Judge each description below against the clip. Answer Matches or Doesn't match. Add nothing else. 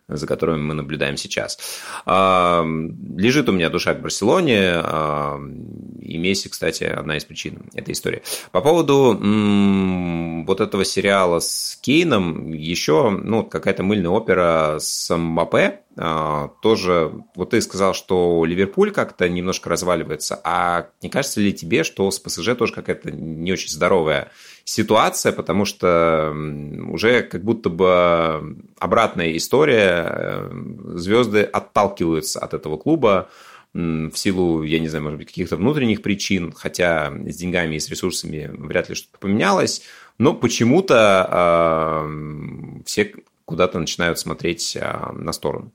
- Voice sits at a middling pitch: Doesn't match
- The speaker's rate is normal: Matches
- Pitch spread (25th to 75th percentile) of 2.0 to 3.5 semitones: Matches